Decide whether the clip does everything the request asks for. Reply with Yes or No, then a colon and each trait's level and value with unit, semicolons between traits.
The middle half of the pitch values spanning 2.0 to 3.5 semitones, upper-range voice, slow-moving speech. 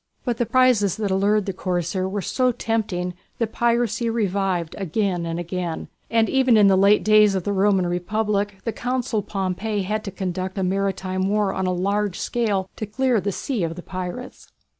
No: average, 2.9 semitones; high, 200 Hz; average, 185 wpm